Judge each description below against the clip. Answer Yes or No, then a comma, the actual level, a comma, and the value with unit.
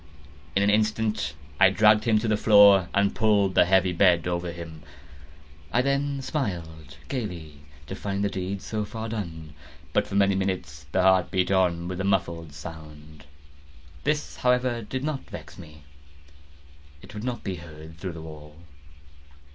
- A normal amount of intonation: Yes, average, 4.6 semitones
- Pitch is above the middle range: No, very low, 95 Hz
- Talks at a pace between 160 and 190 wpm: Yes, average, 165 wpm